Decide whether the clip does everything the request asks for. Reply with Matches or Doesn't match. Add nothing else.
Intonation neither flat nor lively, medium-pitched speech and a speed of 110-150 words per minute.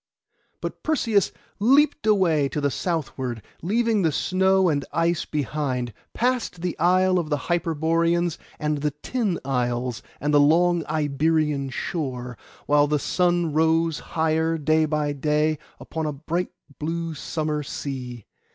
Matches